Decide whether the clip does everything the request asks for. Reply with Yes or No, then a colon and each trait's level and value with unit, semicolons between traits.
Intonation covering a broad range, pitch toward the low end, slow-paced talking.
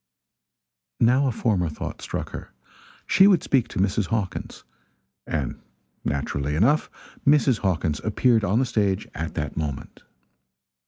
Yes: wide, 7.6 semitones; low, 105 Hz; slow, 130 wpm